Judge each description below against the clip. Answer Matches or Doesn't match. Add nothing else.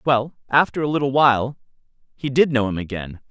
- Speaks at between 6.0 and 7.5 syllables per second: Doesn't match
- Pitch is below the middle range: Matches